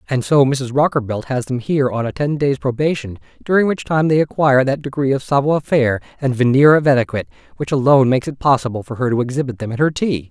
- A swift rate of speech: Yes, fast, 225 wpm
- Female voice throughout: No, male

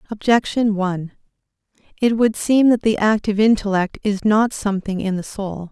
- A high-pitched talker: Yes, high, 210 Hz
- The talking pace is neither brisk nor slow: Yes, average, 160 wpm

